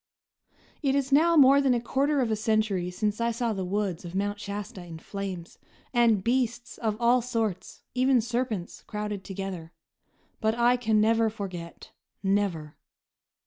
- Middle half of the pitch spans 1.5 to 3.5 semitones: No, average, 3.9 semitones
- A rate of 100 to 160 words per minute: Yes, average, 155 wpm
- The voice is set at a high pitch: Yes, high, 215 Hz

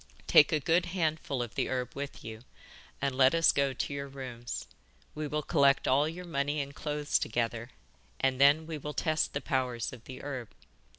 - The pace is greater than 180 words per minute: Yes, average, 190 wpm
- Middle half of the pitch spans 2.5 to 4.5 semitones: Yes, average, 2.8 semitones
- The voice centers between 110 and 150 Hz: Yes, medium, 140 Hz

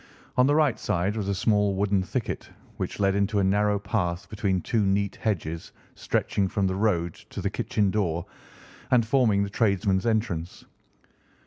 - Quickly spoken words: No, average, 170 wpm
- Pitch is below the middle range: Yes, low, 100 Hz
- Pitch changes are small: Yes, narrow, 2.2 semitones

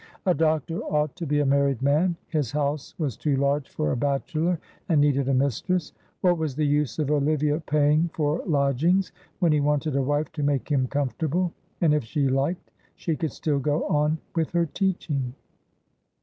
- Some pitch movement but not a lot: No, narrow, 2.3 semitones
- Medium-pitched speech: Yes, medium, 150 Hz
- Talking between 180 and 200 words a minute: Yes, average, 185 wpm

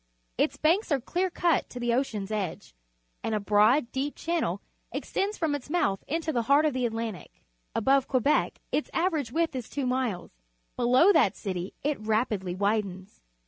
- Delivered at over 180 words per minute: No, average, 170 wpm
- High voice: Yes, very high, 250 Hz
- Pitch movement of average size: No, wide, 6.2 semitones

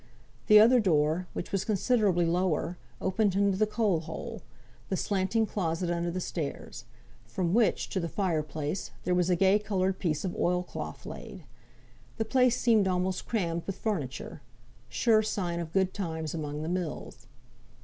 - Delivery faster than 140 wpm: Yes, average, 165 wpm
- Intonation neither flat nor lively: Yes, average, 3.6 semitones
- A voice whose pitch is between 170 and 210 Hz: Yes, medium, 185 Hz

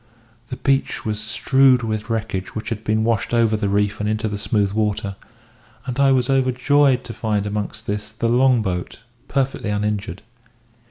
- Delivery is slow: No, average, 170 wpm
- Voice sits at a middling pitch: No, low, 110 Hz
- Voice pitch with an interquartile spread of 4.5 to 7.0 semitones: No, average, 3.2 semitones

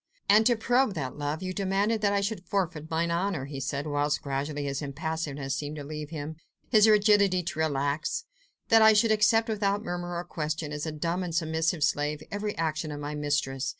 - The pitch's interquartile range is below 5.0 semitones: No, wide, 5.4 semitones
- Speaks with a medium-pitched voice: Yes, medium, 160 Hz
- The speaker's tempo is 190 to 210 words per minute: Yes, average, 200 wpm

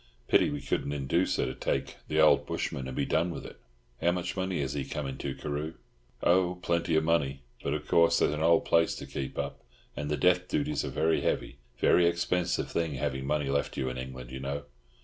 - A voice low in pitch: Yes, very low, 75 Hz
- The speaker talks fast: Yes, fast, 220 wpm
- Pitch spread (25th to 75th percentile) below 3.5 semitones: No, average, 3.8 semitones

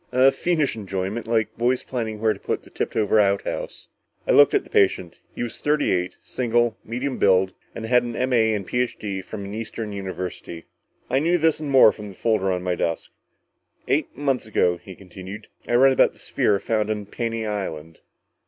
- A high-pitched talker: No, low, 110 Hz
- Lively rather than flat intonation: No, average, 4.1 semitones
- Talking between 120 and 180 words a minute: No, average, 190 wpm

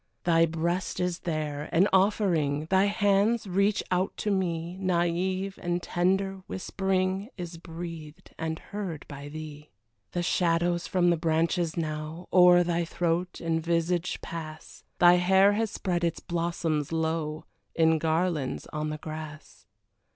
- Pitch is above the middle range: No, medium, 170 Hz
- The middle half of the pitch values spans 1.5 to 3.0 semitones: Yes, narrow, 2.5 semitones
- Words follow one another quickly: No, slow, 135 wpm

